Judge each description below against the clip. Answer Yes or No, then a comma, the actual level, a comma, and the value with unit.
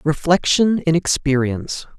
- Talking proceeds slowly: Yes, slow, 90 wpm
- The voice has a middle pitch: Yes, medium, 155 Hz